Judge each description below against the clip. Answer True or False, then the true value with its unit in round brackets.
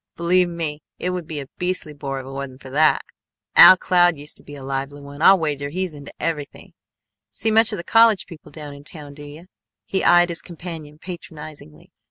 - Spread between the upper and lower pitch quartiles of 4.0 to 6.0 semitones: False (3.6 semitones)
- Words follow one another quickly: True (210 wpm)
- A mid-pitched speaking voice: True (155 Hz)